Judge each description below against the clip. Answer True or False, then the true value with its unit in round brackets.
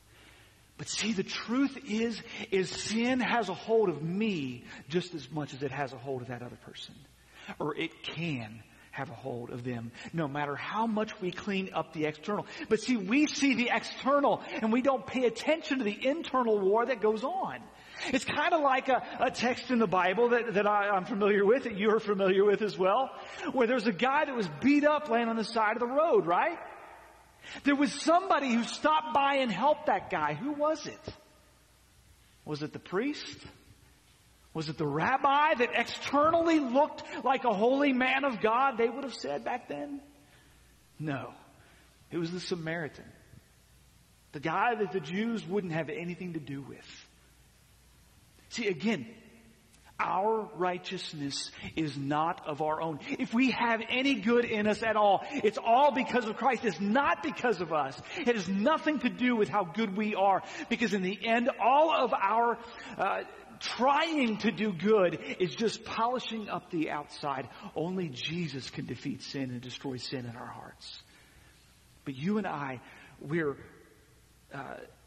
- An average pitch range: False (7.9 semitones)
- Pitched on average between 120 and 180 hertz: False (215 Hz)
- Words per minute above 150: True (175 wpm)